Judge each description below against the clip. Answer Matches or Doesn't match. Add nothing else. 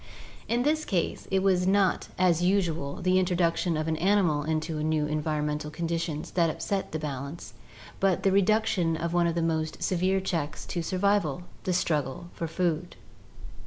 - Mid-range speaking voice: Matches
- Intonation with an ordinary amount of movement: Matches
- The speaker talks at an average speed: Matches